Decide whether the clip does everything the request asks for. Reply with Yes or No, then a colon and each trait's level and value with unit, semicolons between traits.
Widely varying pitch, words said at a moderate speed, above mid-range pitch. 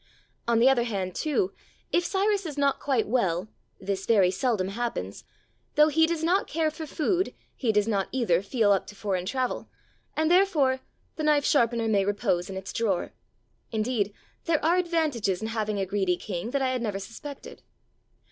Yes: wide, 7.2 semitones; average, 180 wpm; high, 235 Hz